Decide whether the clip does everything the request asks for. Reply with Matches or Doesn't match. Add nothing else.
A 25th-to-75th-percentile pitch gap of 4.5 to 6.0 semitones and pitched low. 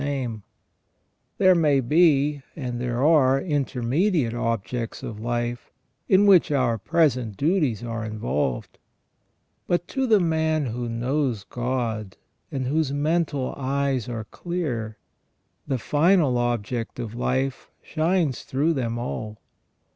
Matches